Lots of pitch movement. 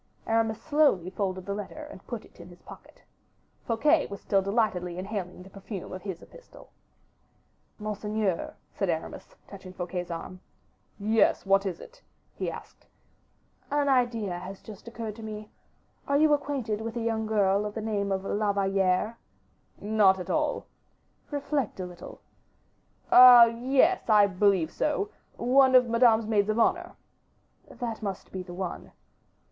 No: average, 3.6 semitones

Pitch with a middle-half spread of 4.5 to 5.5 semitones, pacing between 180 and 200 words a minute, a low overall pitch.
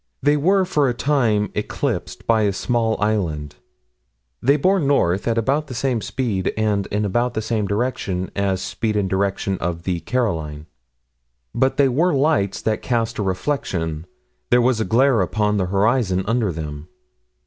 No: average, 5.1 semitones; average, 165 wpm; low, 110 Hz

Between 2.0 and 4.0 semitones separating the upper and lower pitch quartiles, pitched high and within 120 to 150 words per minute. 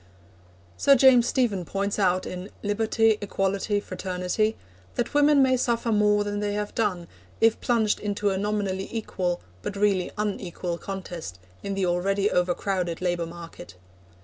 Yes: average, 2.8 semitones; high, 200 Hz; average, 145 wpm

